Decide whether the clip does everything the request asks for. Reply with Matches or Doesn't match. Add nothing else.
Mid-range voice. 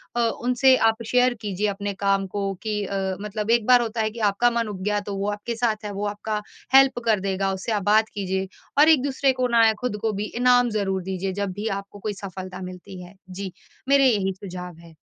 Doesn't match